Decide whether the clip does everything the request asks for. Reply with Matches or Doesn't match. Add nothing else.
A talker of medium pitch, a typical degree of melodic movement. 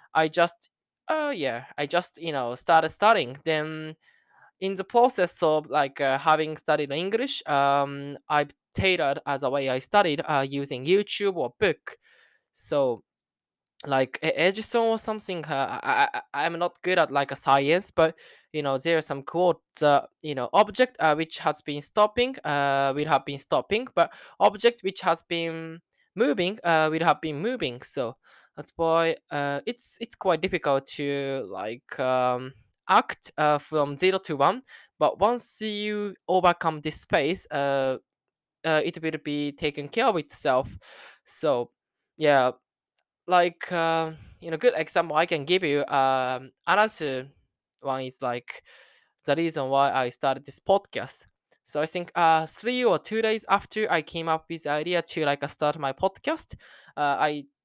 Matches